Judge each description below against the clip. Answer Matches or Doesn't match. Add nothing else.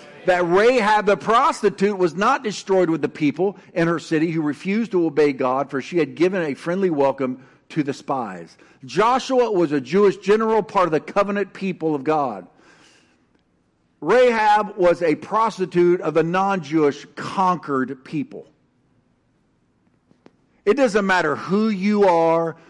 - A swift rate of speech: Doesn't match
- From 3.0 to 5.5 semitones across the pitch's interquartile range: Matches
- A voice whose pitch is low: Doesn't match